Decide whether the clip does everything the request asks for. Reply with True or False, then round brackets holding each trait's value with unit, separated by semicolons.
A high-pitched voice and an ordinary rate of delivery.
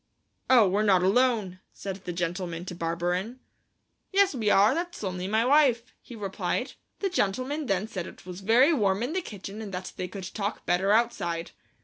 True (200 Hz; 185 wpm)